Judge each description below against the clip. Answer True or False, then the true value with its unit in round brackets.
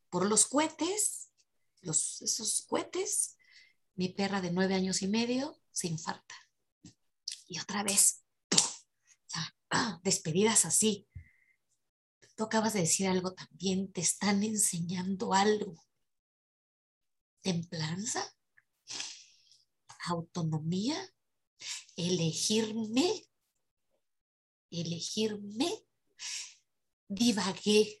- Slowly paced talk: True (75 wpm)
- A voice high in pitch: True (200 Hz)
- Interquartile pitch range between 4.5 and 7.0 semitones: False (3.7 semitones)